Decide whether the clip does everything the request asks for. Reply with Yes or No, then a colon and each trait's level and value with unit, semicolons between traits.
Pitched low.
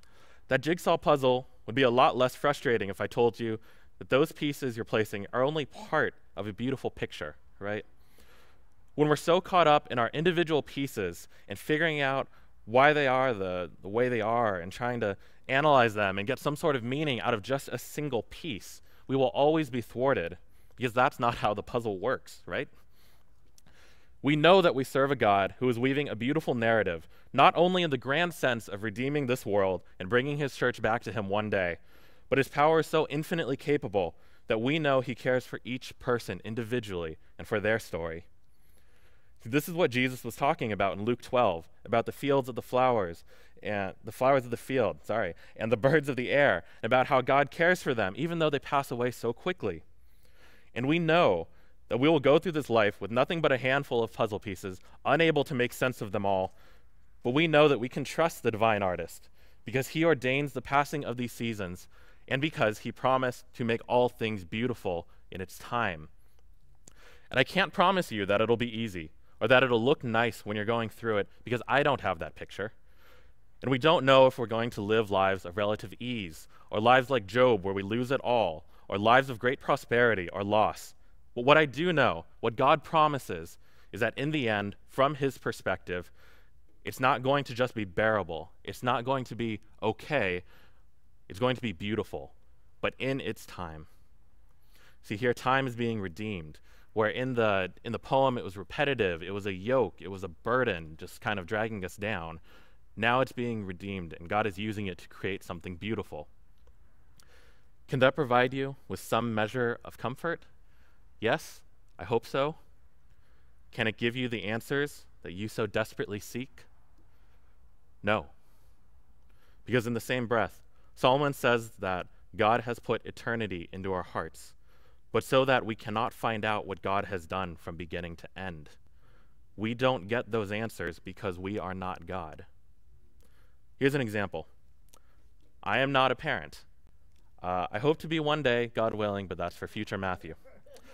Yes: low, 115 Hz